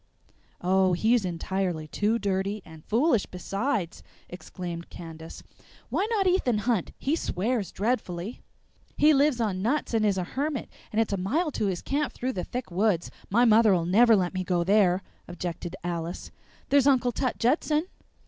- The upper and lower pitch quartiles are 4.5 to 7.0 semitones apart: Yes, wide, 5.6 semitones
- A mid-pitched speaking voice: No, high, 205 Hz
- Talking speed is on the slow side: No, average, 160 wpm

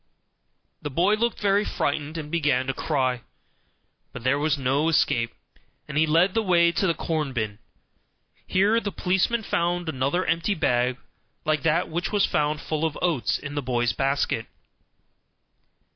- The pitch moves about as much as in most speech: Yes, average, 4.6 semitones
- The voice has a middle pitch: Yes, medium, 155 Hz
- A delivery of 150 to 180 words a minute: Yes, average, 160 wpm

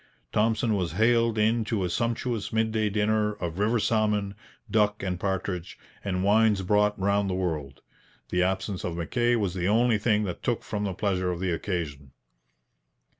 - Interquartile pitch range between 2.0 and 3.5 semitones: Yes, average, 3.1 semitones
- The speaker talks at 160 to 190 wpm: Yes, average, 170 wpm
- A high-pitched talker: No, low, 105 Hz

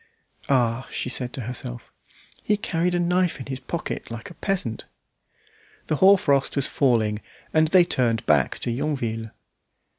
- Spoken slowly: No, average, 155 wpm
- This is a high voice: No, low, 135 Hz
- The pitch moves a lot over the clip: Yes, wide, 6.6 semitones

